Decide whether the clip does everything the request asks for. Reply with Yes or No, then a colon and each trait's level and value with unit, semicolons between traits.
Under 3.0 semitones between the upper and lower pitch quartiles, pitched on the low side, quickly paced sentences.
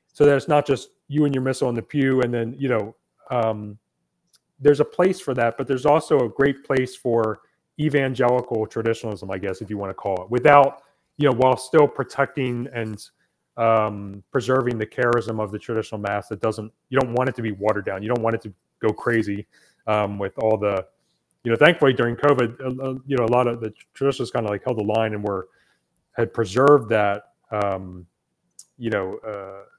No: average, 3.9 semitones; low, 120 Hz; fast, 210 wpm